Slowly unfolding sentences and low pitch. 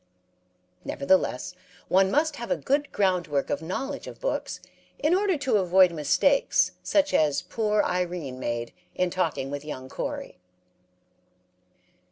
No: slow, 130 wpm; medium, 185 Hz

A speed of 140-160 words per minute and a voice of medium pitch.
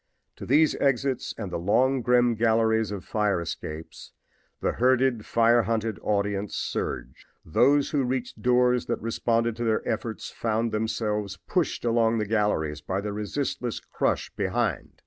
No: average, 145 wpm; low, 115 Hz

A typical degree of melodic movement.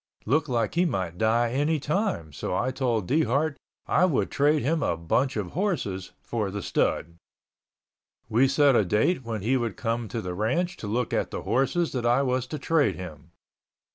No: wide, 5.7 semitones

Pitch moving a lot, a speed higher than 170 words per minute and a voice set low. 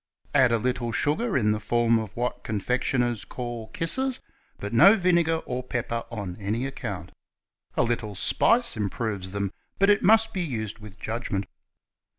No: wide, 5.8 semitones; average, 160 wpm; low, 120 Hz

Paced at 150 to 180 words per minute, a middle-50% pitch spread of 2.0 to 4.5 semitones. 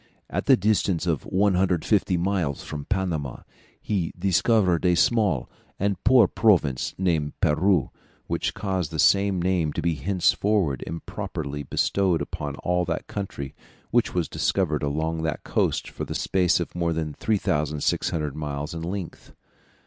No: average, 140 wpm; average, 4.1 semitones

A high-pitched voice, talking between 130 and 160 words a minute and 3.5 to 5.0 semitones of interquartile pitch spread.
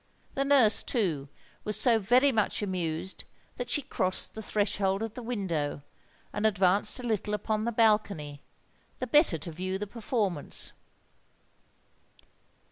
Yes: high, 210 Hz; slow, 135 wpm; average, 3.9 semitones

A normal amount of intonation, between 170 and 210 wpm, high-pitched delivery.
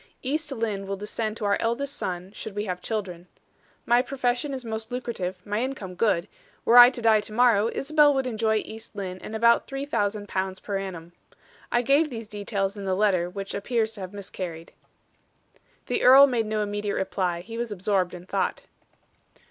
Yes: average, 3.8 semitones; average, 190 wpm; high, 215 Hz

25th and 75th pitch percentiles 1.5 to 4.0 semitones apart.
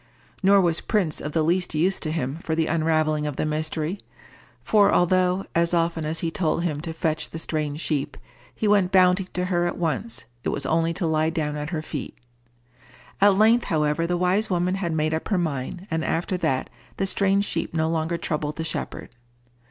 Yes: average, 2.8 semitones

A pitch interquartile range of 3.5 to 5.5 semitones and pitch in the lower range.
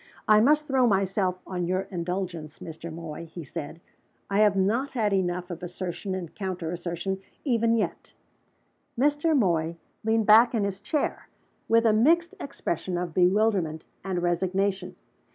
No: average, 4.1 semitones; high, 190 Hz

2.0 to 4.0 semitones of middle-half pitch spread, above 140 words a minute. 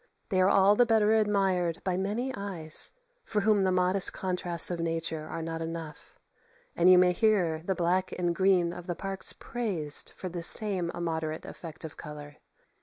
Yes: average, 2.9 semitones; average, 180 wpm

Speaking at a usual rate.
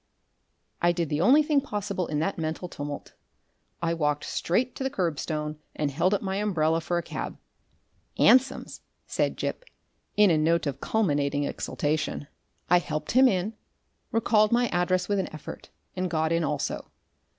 Yes: average, 160 wpm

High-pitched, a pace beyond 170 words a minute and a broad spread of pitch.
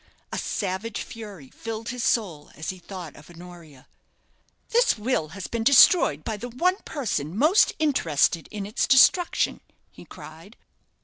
No: high, 210 Hz; average, 145 wpm; wide, 6.7 semitones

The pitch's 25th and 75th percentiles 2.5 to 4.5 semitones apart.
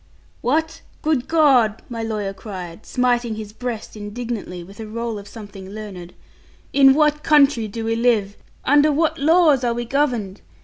No: average, 5.0 semitones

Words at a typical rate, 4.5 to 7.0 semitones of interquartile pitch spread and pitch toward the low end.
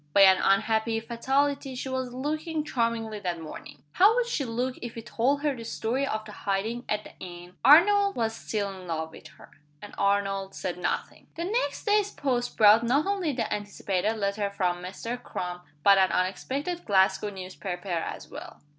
No: average, 180 wpm; wide, 5.5 semitones; high, 225 Hz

